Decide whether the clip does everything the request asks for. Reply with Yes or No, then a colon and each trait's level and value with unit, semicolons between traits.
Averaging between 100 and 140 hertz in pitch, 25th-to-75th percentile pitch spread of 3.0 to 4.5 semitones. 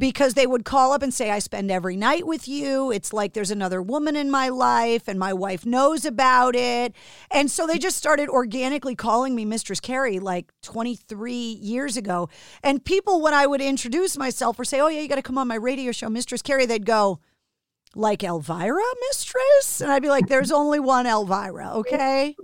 No: very high, 255 Hz; average, 4.1 semitones